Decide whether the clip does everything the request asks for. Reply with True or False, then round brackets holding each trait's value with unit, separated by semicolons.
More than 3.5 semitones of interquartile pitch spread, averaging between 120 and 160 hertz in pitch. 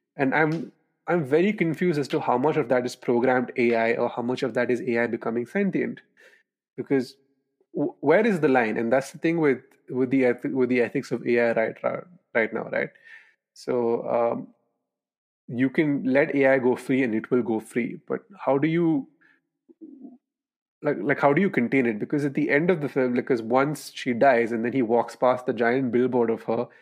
True (4.1 semitones; 135 Hz)